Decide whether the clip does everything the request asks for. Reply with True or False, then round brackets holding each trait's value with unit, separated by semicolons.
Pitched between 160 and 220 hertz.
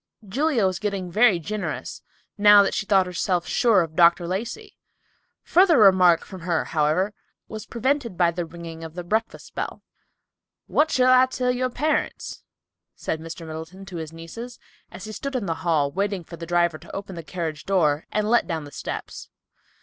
True (185 Hz)